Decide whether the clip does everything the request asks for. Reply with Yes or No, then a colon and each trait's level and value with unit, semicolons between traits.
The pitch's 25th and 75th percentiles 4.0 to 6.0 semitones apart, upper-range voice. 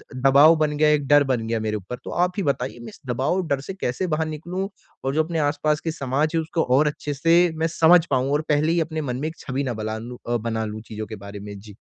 No: average, 4.8 semitones; medium, 145 Hz